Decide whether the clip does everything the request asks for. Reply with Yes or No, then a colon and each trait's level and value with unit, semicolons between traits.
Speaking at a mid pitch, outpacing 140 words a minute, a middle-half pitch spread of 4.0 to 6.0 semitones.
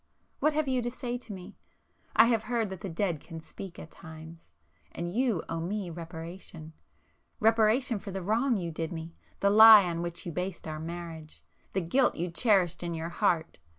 Yes: medium, 180 Hz; average, 170 wpm; average, 4.8 semitones